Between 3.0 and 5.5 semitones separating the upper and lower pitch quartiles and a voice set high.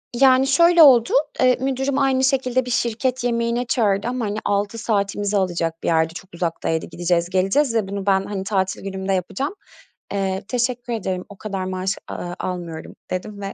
Yes: average, 4.9 semitones; high, 205 Hz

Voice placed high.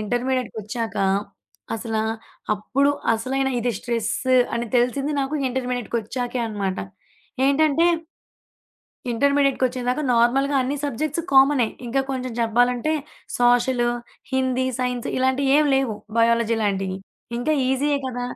Yes: very high, 250 Hz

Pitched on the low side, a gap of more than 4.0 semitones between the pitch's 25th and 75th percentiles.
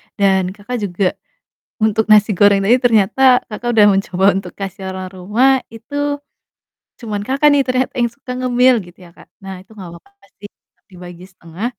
No: high, 210 Hz; average, 4.7 semitones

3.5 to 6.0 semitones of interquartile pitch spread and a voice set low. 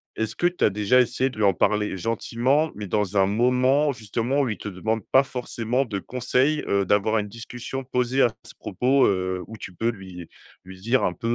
Yes: average, 4.0 semitones; low, 115 Hz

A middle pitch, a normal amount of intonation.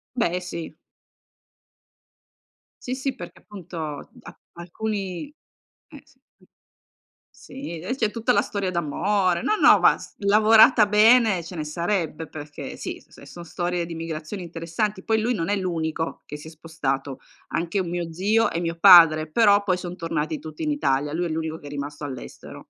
Yes: medium, 175 Hz; average, 4.4 semitones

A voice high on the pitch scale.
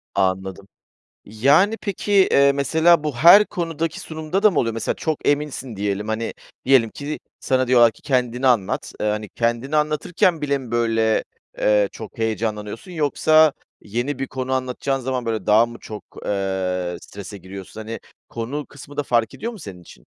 No: low, 125 Hz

